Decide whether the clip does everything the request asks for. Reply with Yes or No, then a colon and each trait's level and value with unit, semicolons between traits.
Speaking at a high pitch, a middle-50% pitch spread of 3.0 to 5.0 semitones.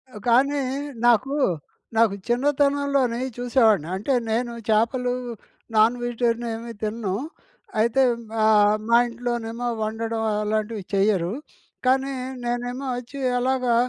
No: high, 235 Hz; narrow, 2.5 semitones